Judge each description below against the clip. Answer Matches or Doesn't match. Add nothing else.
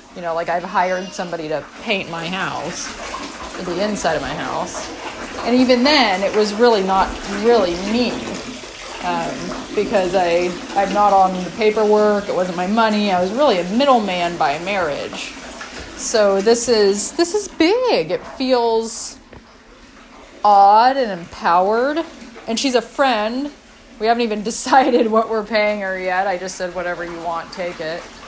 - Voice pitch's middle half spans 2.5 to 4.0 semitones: Doesn't match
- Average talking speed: Matches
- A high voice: Matches